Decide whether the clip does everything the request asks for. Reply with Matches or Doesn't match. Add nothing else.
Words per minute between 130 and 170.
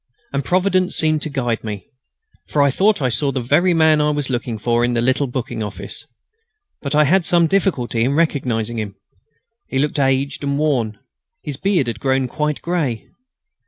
Doesn't match